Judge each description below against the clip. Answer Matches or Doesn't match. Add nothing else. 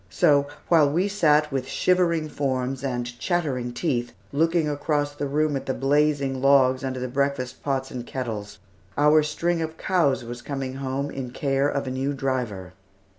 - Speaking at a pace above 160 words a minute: Matches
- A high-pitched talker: Doesn't match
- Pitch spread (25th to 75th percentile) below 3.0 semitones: Matches